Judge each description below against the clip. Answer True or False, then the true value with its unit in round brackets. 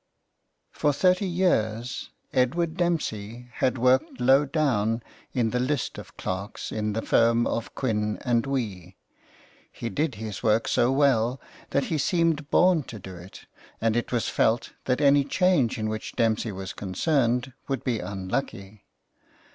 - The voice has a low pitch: True (120 Hz)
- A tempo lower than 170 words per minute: True (150 wpm)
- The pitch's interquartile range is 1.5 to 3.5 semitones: False (4.5 semitones)